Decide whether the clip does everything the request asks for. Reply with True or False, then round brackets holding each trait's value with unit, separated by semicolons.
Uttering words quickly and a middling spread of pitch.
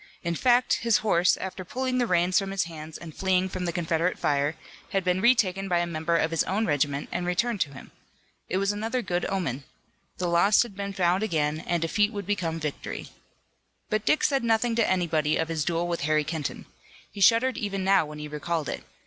True (210 wpm; 4.0 semitones)